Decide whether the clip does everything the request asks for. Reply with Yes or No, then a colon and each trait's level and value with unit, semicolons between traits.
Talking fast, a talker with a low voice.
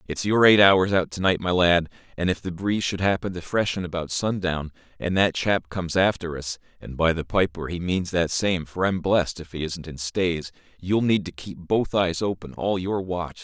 Yes: fast, 220 wpm; very low, 90 Hz